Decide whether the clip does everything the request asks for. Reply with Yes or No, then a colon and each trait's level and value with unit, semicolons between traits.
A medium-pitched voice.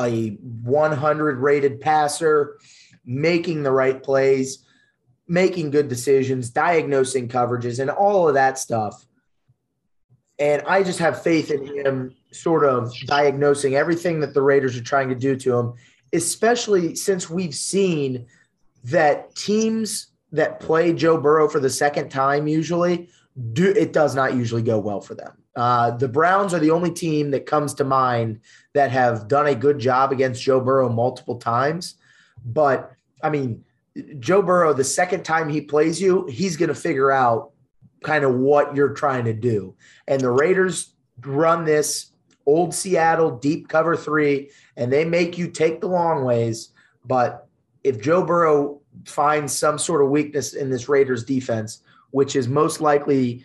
Yes: medium, 145 Hz